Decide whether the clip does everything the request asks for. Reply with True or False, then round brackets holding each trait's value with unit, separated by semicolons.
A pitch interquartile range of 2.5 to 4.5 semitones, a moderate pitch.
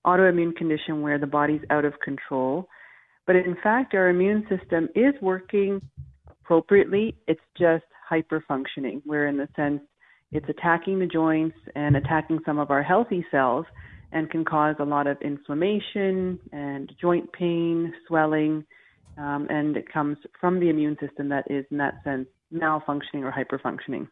True (3.5 semitones; 155 Hz)